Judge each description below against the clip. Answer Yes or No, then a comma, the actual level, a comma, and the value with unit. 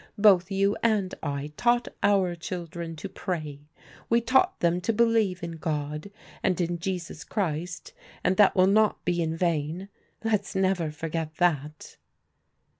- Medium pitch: Yes, medium, 180 Hz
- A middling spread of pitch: Yes, average, 3.6 semitones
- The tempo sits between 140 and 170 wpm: Yes, average, 145 wpm